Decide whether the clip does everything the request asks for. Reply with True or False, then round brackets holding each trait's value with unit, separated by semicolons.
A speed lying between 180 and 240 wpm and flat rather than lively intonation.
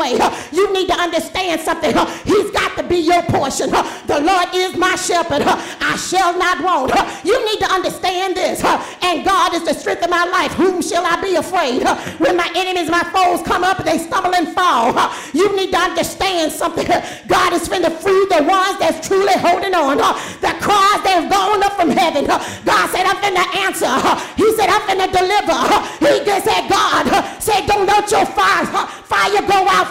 True (190 wpm; 2.1 semitones)